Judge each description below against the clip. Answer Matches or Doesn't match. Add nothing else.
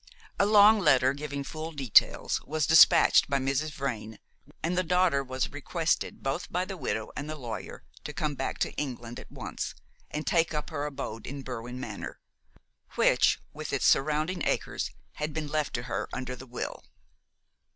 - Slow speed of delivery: Doesn't match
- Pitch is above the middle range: Doesn't match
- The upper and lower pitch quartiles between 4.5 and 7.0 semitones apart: Doesn't match